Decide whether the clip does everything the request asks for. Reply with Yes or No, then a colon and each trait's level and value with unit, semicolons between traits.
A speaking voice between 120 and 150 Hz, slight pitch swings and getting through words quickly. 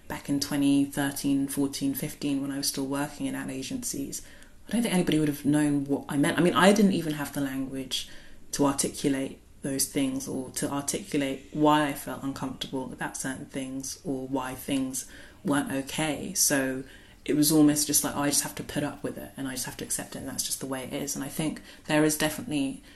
Yes: medium, 140 Hz; narrow, 2.0 semitones; fast, 220 wpm